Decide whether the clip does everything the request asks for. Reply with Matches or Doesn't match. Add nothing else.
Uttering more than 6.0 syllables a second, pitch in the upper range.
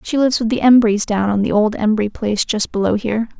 Matches